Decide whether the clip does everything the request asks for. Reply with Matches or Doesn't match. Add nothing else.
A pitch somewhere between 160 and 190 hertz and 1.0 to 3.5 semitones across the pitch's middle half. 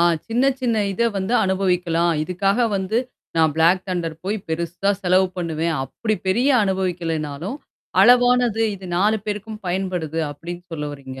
Doesn't match